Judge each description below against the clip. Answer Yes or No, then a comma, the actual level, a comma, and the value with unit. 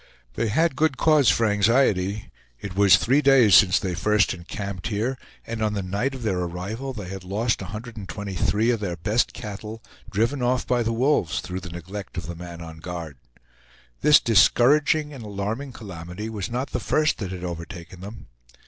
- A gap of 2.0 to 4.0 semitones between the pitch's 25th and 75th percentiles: No, average, 4.7 semitones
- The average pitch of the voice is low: Yes, low, 105 Hz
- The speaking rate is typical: Yes, average, 180 wpm